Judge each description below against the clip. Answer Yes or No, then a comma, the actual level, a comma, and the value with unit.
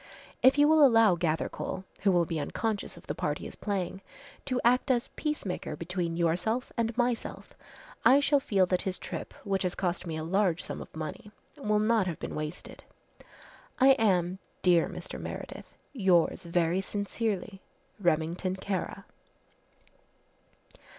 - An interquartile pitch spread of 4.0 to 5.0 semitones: Yes, average, 4.6 semitones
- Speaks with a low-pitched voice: No, high, 190 Hz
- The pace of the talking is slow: No, average, 150 wpm